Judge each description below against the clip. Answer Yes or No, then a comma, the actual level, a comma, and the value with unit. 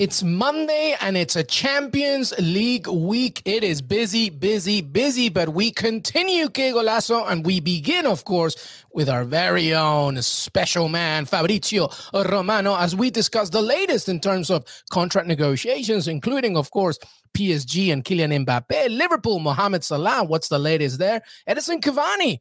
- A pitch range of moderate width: No, wide, 5.8 semitones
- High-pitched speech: Yes, high, 195 Hz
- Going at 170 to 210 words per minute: No, average, 155 wpm